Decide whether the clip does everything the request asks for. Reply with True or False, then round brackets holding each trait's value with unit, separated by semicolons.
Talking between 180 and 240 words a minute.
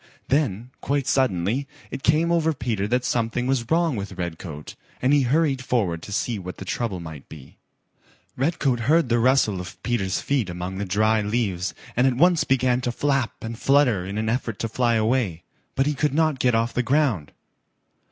True (190 wpm)